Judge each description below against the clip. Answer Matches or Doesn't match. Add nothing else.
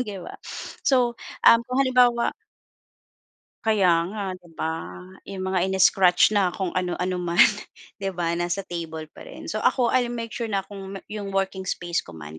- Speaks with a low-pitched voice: Doesn't match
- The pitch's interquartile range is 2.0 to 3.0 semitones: Doesn't match